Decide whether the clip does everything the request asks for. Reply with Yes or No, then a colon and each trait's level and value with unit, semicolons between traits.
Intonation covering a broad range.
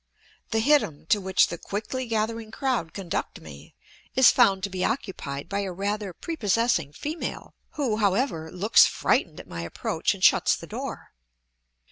No: average, 4.9 semitones